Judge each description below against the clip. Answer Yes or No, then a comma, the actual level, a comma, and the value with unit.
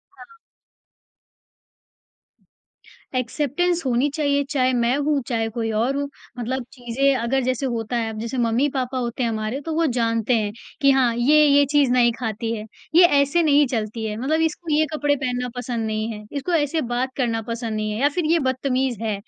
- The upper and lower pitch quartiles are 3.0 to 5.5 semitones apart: Yes, average, 3.8 semitones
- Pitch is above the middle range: Yes, very high, 255 Hz